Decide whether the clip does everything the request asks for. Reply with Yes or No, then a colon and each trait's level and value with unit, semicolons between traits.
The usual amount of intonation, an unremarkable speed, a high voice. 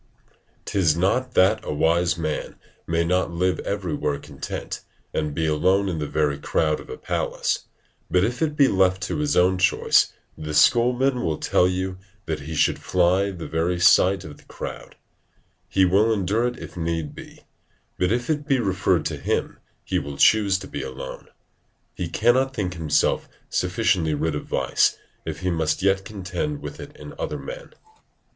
No: average, 4.1 semitones; average, 175 wpm; very low, 90 Hz